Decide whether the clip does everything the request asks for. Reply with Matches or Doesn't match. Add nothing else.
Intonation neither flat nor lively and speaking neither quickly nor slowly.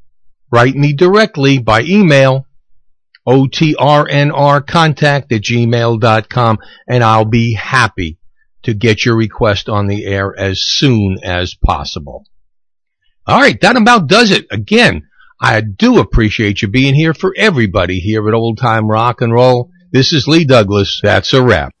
Matches